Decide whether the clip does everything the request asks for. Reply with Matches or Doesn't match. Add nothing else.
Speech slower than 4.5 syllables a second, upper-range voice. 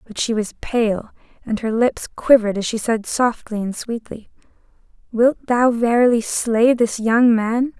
Matches